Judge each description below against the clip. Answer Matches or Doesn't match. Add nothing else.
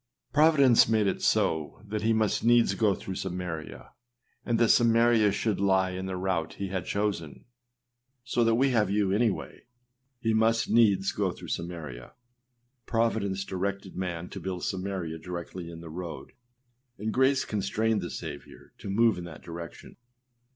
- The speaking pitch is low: Matches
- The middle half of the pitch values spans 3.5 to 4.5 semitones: Matches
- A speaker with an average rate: Matches